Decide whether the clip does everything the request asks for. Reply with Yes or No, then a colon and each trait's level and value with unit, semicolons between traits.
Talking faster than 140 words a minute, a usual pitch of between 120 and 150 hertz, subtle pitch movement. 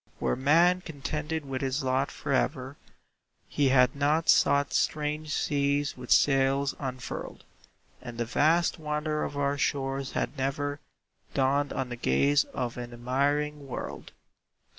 No: slow, 135 wpm; medium, 140 Hz; narrow, 2.1 semitones